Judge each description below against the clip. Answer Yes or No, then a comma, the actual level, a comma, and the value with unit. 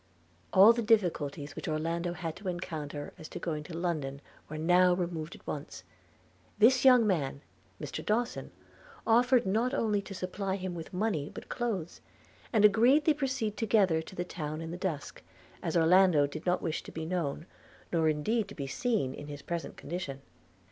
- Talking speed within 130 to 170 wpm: No, average, 185 wpm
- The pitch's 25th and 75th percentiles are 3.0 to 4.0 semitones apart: No, average, 5.2 semitones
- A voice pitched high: No, medium, 180 Hz